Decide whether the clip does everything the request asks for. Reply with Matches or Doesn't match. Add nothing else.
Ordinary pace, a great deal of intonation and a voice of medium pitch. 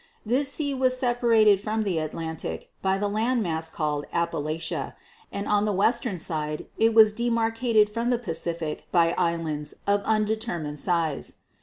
Doesn't match